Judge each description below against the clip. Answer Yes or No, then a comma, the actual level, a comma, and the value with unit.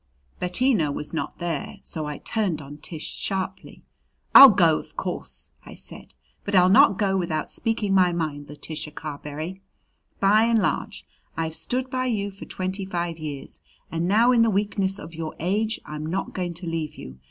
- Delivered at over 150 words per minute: Yes, average, 175 wpm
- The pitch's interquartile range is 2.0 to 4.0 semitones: No, average, 4.4 semitones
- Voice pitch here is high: No, medium, 180 Hz